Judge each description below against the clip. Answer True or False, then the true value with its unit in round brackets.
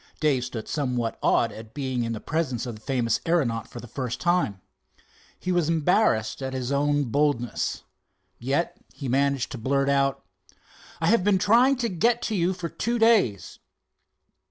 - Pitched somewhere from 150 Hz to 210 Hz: False (140 Hz)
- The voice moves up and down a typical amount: False (6.1 semitones)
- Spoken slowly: False (170 wpm)